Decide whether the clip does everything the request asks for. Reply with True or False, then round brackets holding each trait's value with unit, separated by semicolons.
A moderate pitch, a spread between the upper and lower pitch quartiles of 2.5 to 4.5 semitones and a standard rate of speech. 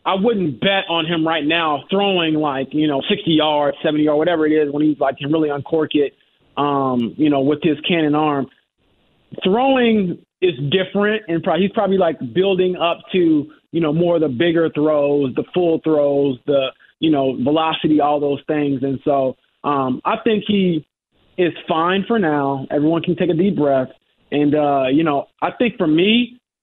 True (155 Hz; 4.0 semitones; 190 wpm)